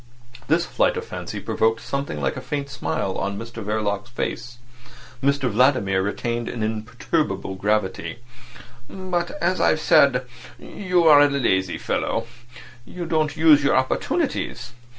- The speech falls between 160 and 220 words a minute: No, slow, 135 wpm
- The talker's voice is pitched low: Yes, low, 125 Hz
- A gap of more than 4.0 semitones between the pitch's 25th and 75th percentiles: Yes, wide, 5.6 semitones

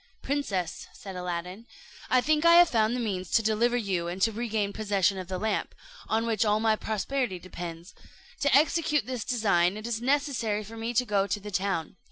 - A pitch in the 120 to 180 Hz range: No, high, 215 Hz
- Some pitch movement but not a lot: Yes, average, 4.1 semitones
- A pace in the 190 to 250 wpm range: Yes, average, 200 wpm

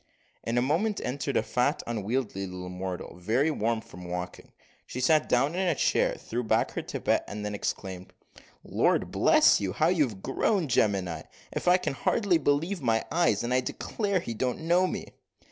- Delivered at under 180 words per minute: No, average, 185 wpm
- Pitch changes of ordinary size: No, wide, 7.7 semitones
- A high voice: No, low, 125 Hz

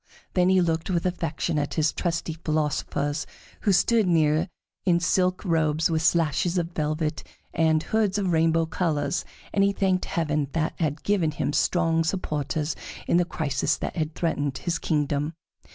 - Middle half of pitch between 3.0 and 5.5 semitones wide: No, narrow, 2.6 semitones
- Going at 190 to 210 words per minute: No, average, 160 wpm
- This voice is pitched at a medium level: Yes, medium, 165 Hz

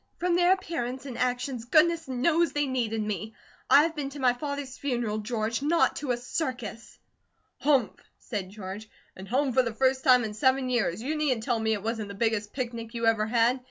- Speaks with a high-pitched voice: Yes, high, 245 Hz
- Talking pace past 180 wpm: Yes, average, 200 wpm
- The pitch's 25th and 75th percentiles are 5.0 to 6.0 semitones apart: No, average, 3.8 semitones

